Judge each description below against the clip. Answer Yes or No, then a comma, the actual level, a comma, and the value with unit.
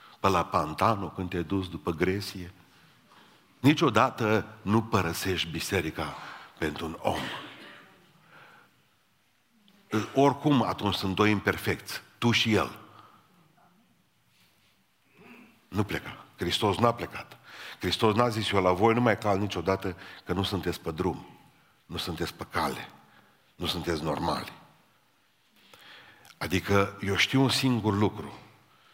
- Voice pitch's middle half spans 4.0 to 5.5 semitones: No, average, 3.5 semitones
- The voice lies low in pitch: Yes, low, 100 Hz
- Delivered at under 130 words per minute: Yes, slow, 115 wpm